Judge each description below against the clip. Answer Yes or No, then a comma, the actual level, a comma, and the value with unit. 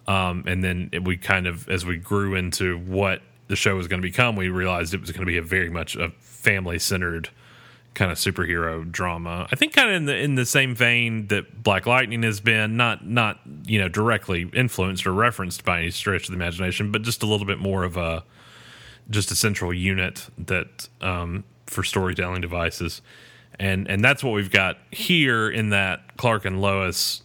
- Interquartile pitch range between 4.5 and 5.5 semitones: No, average, 3.7 semitones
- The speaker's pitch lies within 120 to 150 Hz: No, very low, 95 Hz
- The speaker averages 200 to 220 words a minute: Yes, fast, 205 wpm